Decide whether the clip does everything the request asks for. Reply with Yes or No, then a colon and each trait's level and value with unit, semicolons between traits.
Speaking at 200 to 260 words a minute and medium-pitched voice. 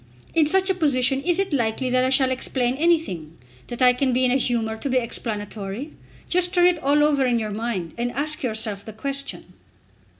No: fast, 205 wpm; very high, 255 Hz